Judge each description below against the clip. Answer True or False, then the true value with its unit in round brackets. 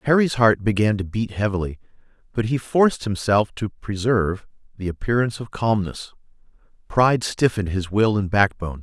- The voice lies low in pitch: True (105 Hz)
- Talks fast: False (150 wpm)